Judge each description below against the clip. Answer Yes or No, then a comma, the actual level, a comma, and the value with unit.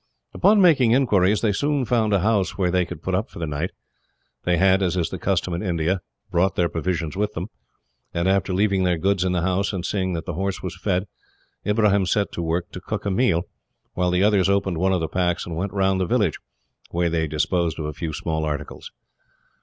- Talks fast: Yes, fast, 225 wpm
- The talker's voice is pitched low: Yes, very low, 95 Hz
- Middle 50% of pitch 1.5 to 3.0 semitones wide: Yes, average, 2.7 semitones